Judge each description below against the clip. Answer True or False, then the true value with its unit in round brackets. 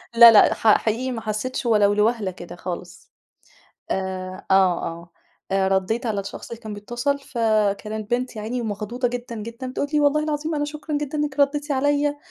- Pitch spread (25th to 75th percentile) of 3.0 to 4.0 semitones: False (5.3 semitones)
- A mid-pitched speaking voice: False (230 Hz)